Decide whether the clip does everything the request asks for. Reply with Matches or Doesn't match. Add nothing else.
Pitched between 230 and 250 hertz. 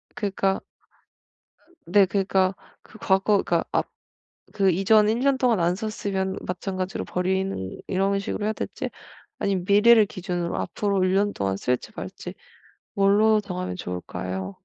Doesn't match